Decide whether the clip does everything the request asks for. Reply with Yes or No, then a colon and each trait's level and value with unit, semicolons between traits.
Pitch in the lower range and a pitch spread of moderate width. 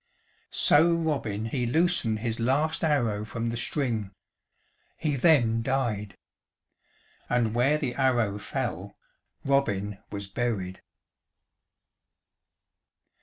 Yes: low, 120 Hz; average, 4.4 semitones